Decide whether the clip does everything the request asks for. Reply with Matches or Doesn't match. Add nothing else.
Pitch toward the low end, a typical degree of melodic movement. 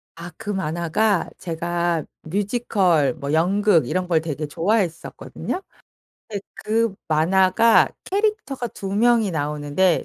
Doesn't match